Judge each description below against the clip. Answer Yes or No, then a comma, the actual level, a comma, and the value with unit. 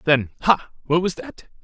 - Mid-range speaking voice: Yes, medium, 155 Hz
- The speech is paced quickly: No, average, 145 wpm